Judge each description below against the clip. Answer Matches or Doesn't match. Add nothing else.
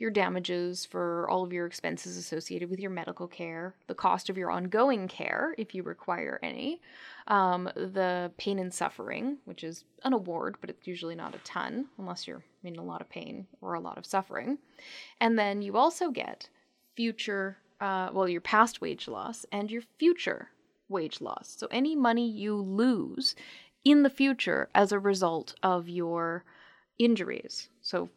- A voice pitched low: Doesn't match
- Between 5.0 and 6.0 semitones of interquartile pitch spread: Matches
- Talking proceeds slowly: Doesn't match